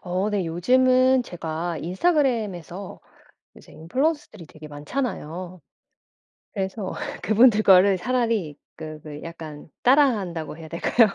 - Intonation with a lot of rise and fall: Yes, wide, 6.7 semitones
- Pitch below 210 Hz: Yes, high, 190 Hz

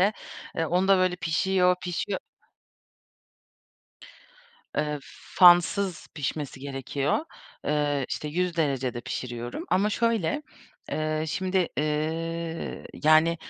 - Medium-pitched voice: Yes, medium, 165 Hz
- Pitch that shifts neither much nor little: Yes, average, 3.5 semitones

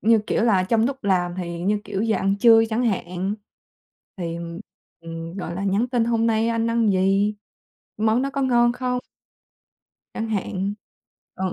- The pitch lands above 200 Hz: Yes, high, 215 Hz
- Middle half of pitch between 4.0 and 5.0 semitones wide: No, average, 3.4 semitones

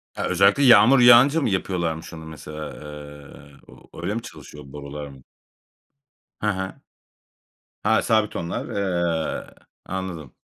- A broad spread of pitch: Yes, wide, 6.3 semitones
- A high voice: No, very low, 85 Hz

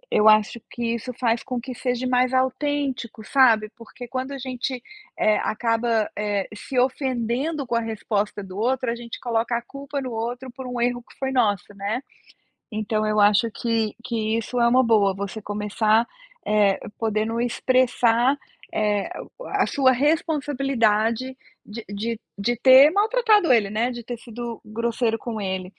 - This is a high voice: Yes, high, 235 Hz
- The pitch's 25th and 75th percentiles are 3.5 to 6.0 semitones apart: No, average, 3.1 semitones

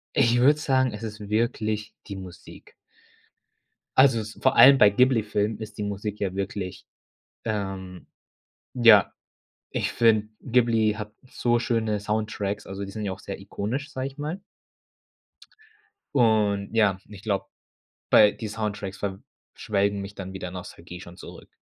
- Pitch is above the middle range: No, low, 105 Hz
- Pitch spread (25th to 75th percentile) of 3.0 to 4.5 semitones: No, narrow, 2.5 semitones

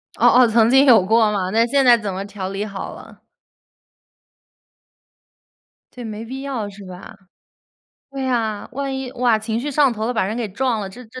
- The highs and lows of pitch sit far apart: No, average, 3.5 semitones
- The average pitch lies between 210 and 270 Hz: Yes, high, 225 Hz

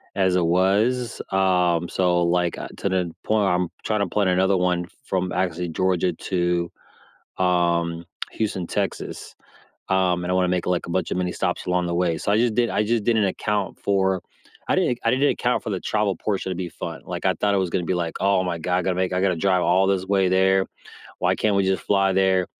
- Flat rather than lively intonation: Yes, narrow, 1.7 semitones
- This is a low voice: Yes, very low, 95 Hz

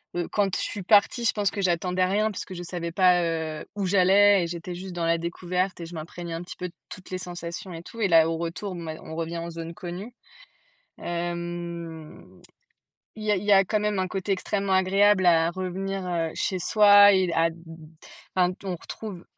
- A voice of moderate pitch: Yes, medium, 180 Hz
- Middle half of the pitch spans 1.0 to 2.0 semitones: No, narrow, 2.5 semitones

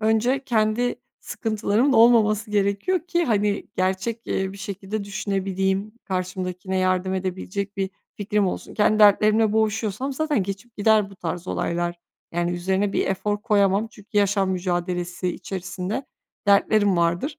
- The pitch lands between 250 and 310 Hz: No, high, 200 Hz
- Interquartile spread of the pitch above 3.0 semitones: No, narrow, 2.5 semitones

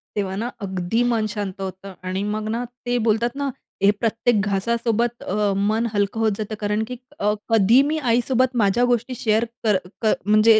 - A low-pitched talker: No, high, 220 Hz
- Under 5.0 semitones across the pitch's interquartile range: Yes, average, 2.8 semitones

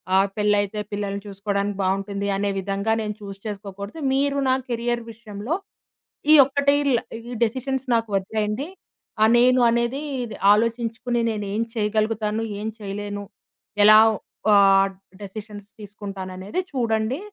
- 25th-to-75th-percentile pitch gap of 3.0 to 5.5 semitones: No, narrow, 2.6 semitones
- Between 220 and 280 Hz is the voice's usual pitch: No, high, 210 Hz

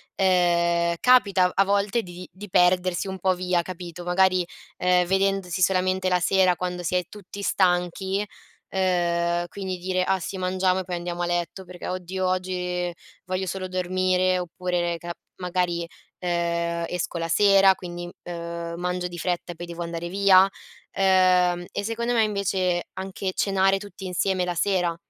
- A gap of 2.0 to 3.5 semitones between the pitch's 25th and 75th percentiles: No, narrow, 1.4 semitones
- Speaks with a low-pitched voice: No, medium, 180 Hz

